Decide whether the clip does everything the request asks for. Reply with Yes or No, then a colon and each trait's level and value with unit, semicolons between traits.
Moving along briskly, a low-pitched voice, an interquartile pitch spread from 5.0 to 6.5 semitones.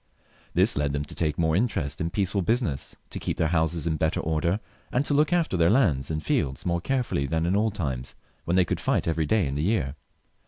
Yes: fast, 235 wpm; very low, 85 Hz; wide, 5.4 semitones